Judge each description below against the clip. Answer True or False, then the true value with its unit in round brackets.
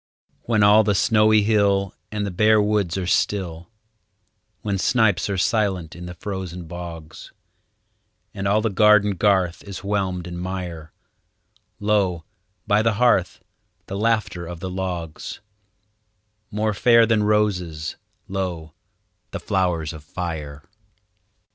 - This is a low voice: True (95 Hz)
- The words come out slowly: True (130 wpm)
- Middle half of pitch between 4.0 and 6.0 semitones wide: False (3.3 semitones)